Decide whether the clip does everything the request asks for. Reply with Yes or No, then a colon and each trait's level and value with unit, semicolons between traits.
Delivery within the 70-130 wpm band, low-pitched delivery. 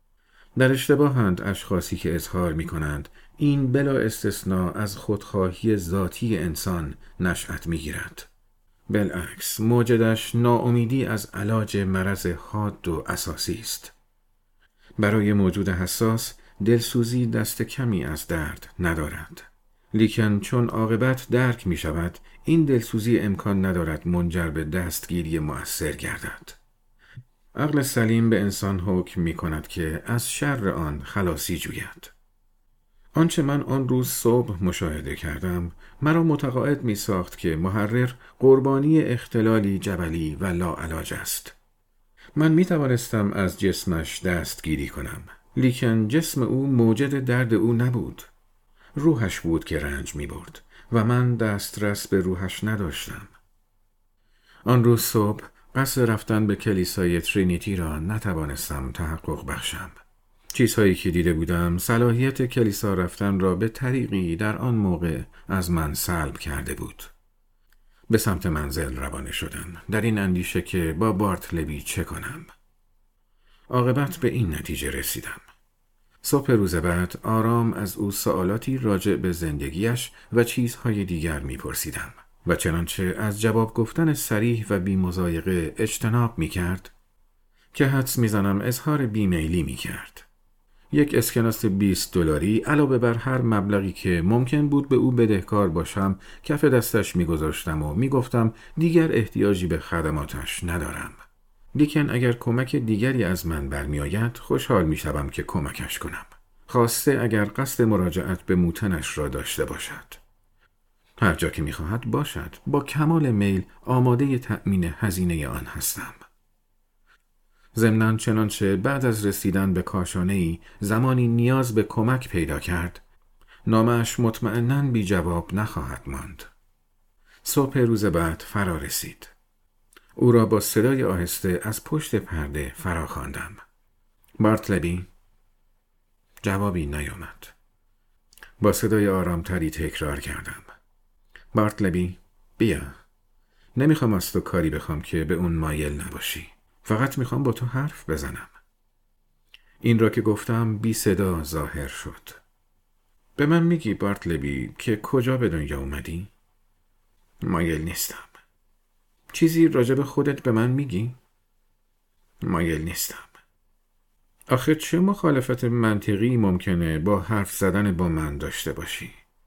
Yes: average, 125 wpm; low, 100 Hz